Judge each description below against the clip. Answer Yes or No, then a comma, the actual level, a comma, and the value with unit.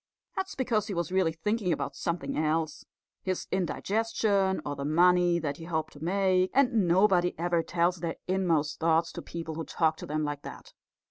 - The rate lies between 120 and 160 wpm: No, average, 185 wpm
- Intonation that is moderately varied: Yes, average, 3.0 semitones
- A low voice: No, medium, 175 Hz